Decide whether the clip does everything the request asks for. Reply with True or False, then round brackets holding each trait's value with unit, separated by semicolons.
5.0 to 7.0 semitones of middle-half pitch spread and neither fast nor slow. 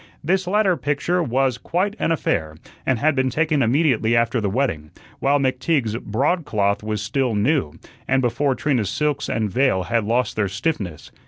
True (5.5 semitones; 165 wpm)